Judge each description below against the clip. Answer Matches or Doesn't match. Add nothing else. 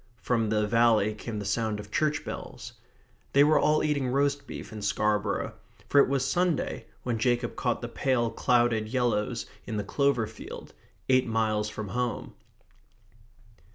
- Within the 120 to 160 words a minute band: Matches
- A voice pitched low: Matches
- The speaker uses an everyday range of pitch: Matches